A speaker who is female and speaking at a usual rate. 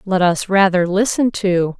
Yes: female; average, 170 wpm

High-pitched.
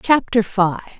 Yes: high, 225 Hz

